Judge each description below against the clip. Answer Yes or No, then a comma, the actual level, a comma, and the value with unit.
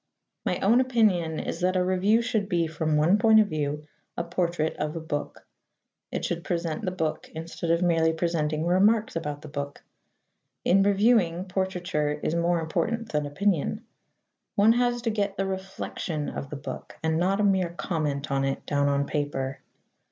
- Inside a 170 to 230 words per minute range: Yes, average, 175 wpm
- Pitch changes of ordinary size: Yes, average, 4.2 semitones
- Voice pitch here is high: No, medium, 170 Hz